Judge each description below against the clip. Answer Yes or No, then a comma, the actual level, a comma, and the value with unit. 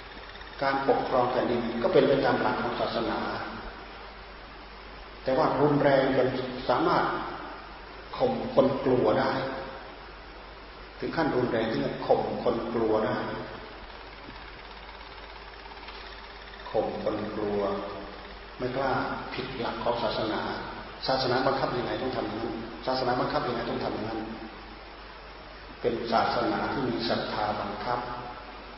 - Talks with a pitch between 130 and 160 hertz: No, low, 120 Hz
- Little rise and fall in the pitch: No, average, 3.2 semitones